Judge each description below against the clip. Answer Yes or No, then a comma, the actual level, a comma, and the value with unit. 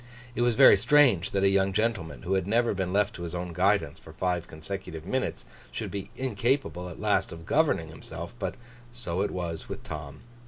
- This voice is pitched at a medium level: No, very low, 95 Hz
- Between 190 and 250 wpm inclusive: Yes, average, 200 wpm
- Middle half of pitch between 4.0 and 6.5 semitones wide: Yes, average, 4.4 semitones